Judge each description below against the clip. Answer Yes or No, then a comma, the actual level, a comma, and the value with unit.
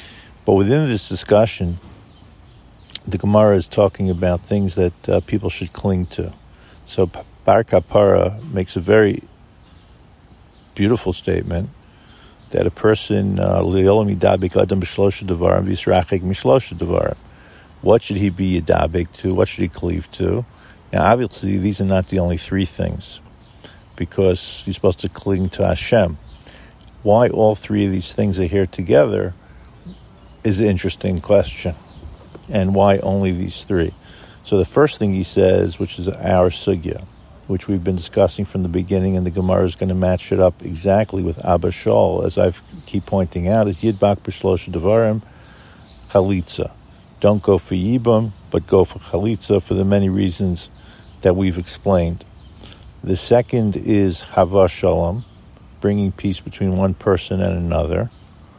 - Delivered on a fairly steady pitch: Yes, narrow, 2.0 semitones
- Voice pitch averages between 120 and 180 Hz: No, very low, 95 Hz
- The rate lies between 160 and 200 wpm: No, average, 145 wpm